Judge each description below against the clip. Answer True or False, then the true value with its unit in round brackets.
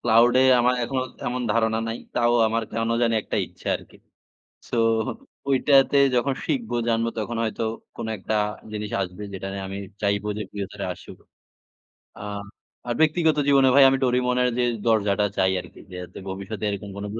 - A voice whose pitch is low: True (115 Hz)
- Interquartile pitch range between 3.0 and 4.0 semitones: True (3.5 semitones)